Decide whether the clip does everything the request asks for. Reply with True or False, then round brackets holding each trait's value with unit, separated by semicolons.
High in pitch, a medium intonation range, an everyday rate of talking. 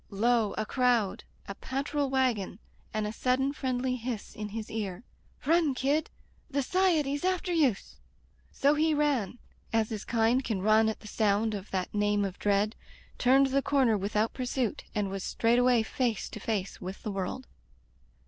True (230 Hz; 4.3 semitones; 165 wpm)